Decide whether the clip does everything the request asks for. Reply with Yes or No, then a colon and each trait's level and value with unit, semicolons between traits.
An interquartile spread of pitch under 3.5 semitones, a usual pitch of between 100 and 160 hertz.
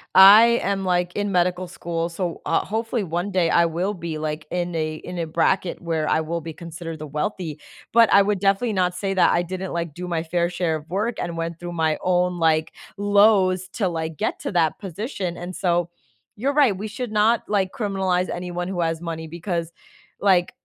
No: average, 2.8 semitones; medium, 180 Hz